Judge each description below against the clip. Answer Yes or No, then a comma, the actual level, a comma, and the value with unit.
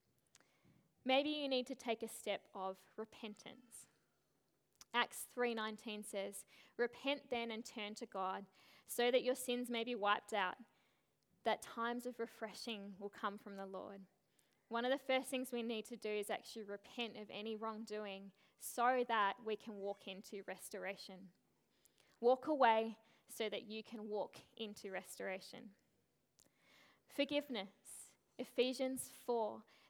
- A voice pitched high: Yes, high, 225 Hz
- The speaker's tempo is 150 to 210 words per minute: No, average, 140 wpm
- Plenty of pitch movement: No, average, 3.2 semitones